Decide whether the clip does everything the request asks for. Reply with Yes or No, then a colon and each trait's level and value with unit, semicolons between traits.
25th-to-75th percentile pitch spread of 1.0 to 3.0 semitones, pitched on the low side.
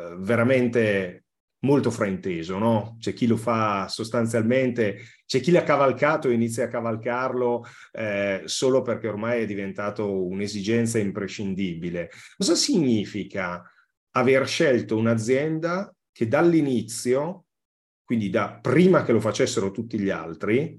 No: average, 4.2 semitones; low, 115 Hz